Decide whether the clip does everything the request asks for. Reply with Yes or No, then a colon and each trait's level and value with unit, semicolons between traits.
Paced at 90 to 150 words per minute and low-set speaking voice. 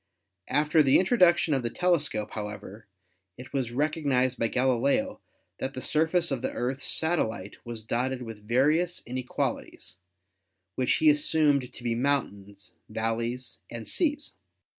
Yes: average, 140 wpm; low, 130 Hz